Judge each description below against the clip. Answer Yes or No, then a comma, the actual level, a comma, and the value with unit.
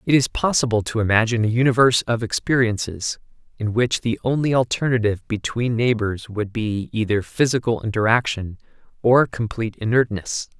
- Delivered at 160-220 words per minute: No, slow, 135 wpm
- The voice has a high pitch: No, low, 115 Hz